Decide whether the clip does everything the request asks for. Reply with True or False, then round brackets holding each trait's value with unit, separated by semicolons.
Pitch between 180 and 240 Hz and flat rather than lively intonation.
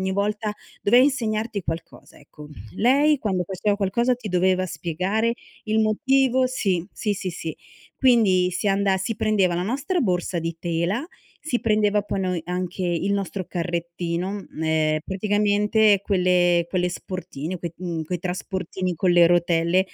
False (190 Hz; 3.4 semitones)